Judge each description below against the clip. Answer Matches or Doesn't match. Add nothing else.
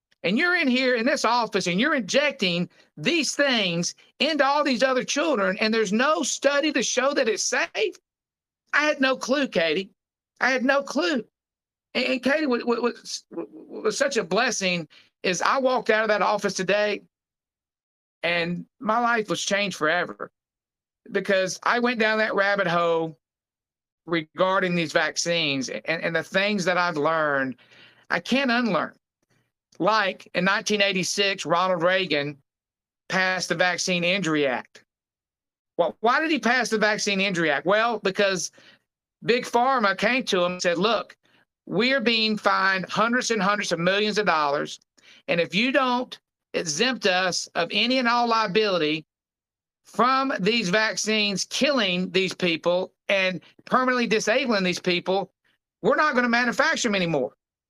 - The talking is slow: Doesn't match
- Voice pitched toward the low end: Doesn't match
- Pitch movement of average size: Doesn't match